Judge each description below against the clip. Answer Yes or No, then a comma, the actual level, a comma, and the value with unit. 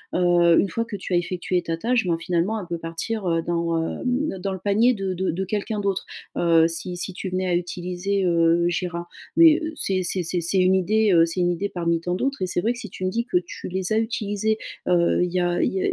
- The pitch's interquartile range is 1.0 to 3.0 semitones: Yes, average, 2.7 semitones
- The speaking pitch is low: No, medium, 180 Hz